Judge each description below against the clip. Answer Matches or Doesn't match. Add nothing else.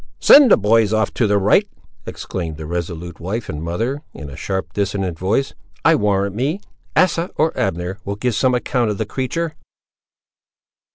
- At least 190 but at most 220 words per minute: Doesn't match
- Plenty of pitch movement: Matches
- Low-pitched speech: Matches